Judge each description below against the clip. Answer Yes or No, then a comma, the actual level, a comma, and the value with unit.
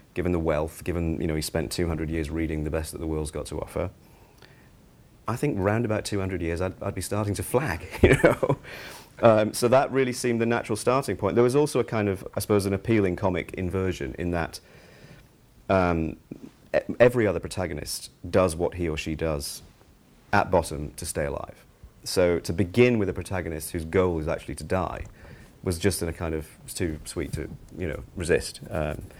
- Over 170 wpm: Yes, fast, 205 wpm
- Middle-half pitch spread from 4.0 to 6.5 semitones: Yes, average, 4.4 semitones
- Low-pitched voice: Yes, very low, 90 Hz